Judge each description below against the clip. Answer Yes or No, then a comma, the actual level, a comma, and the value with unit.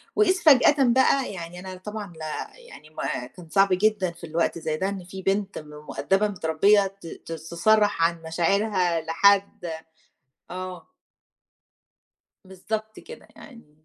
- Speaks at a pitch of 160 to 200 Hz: Yes, high, 190 Hz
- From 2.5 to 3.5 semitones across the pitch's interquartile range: No, average, 4.1 semitones